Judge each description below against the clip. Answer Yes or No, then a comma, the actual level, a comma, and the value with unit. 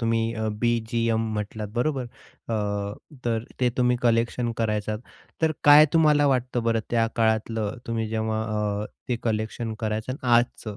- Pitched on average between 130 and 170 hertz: No, low, 115 Hz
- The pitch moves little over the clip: Yes, narrow, 2.0 semitones